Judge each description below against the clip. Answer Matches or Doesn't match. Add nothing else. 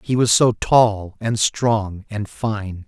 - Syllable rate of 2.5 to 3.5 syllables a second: Matches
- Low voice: Matches